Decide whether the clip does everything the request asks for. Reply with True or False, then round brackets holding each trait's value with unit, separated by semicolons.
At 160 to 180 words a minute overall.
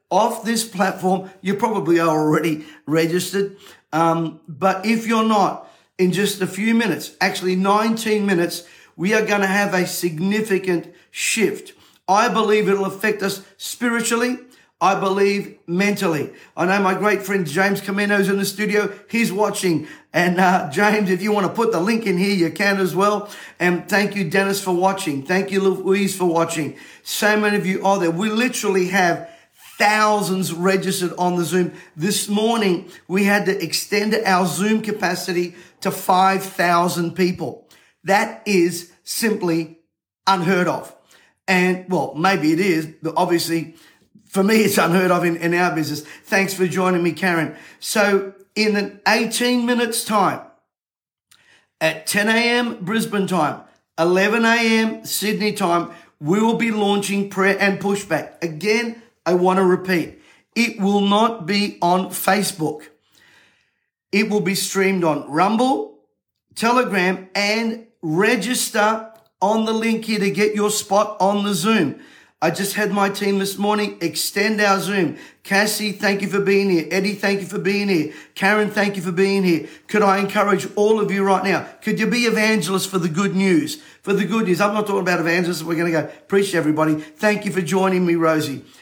True (165 wpm)